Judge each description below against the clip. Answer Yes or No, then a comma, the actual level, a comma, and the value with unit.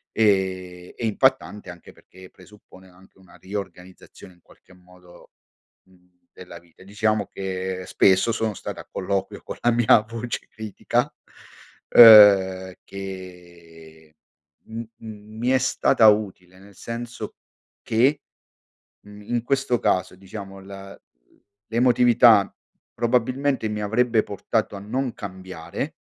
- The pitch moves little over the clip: No, average, 3.4 semitones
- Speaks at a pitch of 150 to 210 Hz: No, low, 100 Hz